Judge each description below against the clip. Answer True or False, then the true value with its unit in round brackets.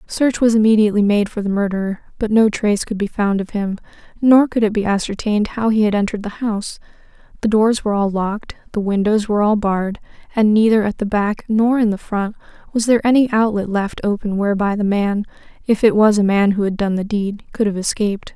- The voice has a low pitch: False (210 Hz)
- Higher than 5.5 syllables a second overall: True (6.0 syllables/s)